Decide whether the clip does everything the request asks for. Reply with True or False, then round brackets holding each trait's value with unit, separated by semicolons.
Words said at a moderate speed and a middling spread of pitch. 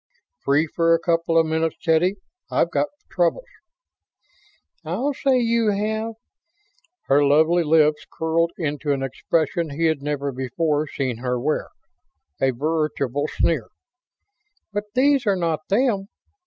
False (130 wpm; 4.9 semitones)